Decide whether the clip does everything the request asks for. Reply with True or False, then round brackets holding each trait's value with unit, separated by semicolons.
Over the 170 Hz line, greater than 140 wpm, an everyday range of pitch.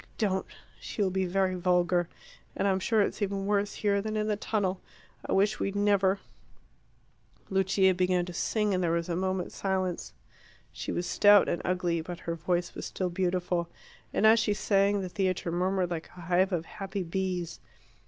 False (190 Hz; 185 wpm; 2.0 semitones)